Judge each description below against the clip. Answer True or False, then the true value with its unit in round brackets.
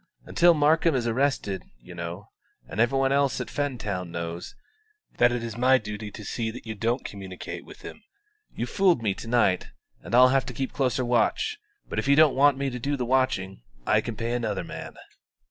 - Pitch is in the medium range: False (120 Hz)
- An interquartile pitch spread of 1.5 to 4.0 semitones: False (4.5 semitones)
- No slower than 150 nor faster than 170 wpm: False (205 wpm)